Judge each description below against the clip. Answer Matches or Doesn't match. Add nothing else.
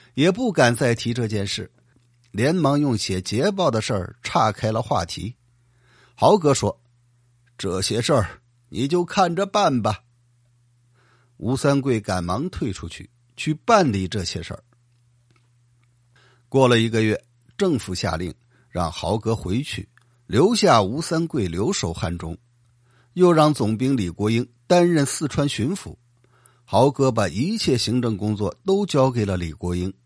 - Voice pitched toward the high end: Doesn't match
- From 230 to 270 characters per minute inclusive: Doesn't match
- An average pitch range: Matches